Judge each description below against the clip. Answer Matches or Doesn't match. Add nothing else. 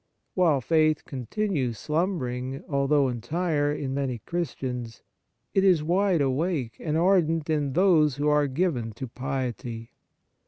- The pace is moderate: Doesn't match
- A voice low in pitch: Doesn't match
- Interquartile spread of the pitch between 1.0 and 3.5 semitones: Doesn't match